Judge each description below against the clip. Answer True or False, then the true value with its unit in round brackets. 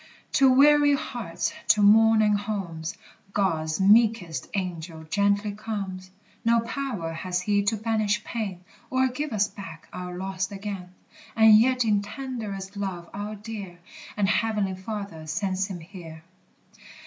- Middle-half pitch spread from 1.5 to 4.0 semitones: True (3.3 semitones)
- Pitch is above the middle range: True (200 Hz)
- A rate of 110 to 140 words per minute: True (135 wpm)